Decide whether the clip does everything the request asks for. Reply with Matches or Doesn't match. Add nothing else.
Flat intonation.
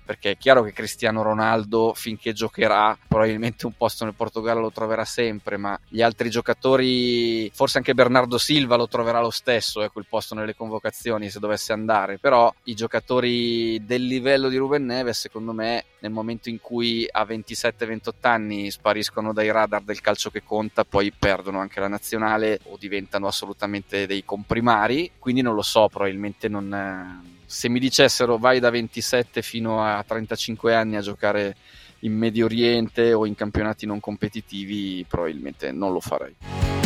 Matches